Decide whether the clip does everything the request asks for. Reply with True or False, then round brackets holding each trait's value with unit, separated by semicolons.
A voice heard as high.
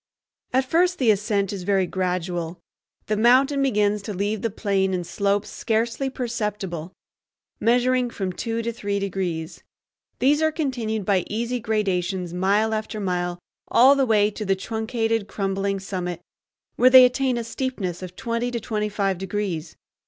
True (210 Hz)